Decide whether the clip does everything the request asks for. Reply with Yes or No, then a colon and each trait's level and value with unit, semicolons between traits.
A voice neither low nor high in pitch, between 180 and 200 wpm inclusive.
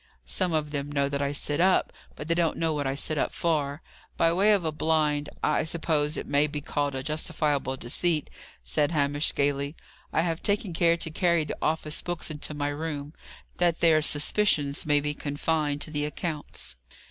Yes: medium, 150 Hz; average, 195 wpm